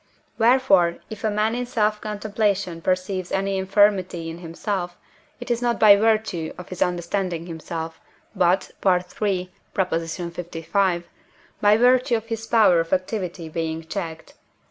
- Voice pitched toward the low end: No, high, 190 Hz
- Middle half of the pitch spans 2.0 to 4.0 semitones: Yes, average, 3.7 semitones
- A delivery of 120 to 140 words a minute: Yes, slow, 135 wpm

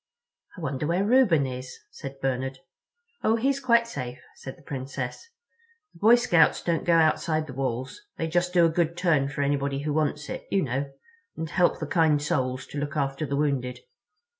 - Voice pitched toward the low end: No, medium, 150 Hz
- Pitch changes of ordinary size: Yes, average, 4.2 semitones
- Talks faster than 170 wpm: Yes, average, 180 wpm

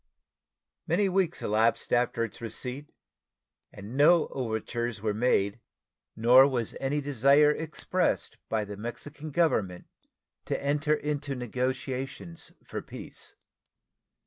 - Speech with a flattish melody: No, average, 4.4 semitones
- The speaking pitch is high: No, low, 130 Hz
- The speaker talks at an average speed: No, slow, 110 wpm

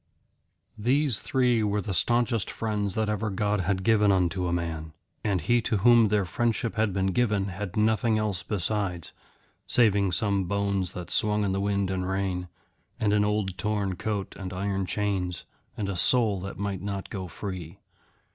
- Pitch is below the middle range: Yes, low, 100 Hz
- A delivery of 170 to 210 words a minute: Yes, average, 175 wpm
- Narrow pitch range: Yes, narrow, 2.3 semitones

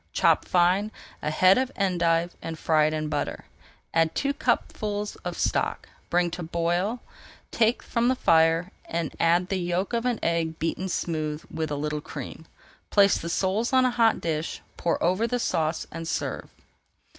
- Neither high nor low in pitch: Yes, medium, 175 Hz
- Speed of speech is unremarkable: Yes, average, 175 wpm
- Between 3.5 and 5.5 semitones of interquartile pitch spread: Yes, average, 4.0 semitones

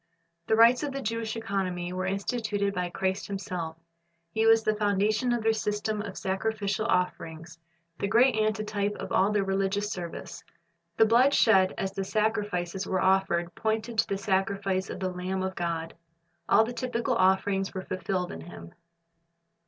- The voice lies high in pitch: Yes, high, 200 Hz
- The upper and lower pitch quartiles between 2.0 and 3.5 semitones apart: Yes, average, 2.7 semitones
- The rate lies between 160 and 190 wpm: Yes, average, 165 wpm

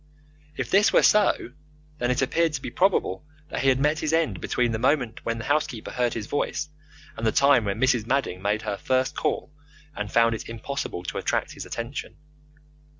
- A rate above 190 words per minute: Yes, average, 200 wpm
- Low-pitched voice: Yes, low, 125 Hz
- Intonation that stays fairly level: No, average, 4.4 semitones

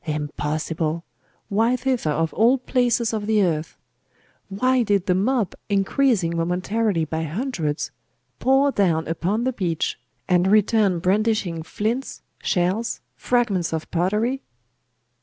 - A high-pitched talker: Yes, high, 200 Hz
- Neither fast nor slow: No, slow, 120 wpm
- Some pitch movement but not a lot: No, wide, 5.7 semitones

